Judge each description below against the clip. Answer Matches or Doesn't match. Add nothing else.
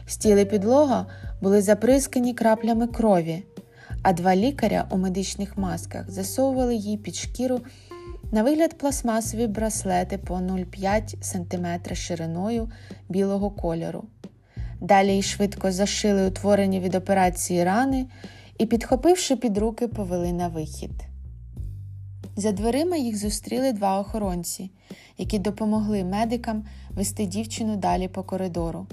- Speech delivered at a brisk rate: Doesn't match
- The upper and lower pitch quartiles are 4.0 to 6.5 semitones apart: Matches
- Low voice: Doesn't match